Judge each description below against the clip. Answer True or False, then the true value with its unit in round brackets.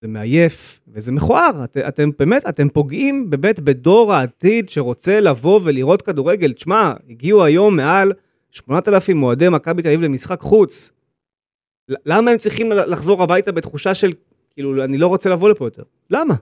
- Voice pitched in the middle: True (170 Hz)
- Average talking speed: False (155 wpm)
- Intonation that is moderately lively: False (6.0 semitones)